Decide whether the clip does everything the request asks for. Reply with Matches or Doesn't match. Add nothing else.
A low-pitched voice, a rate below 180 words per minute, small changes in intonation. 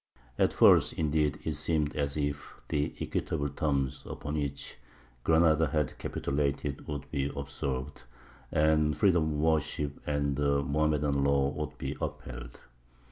Matches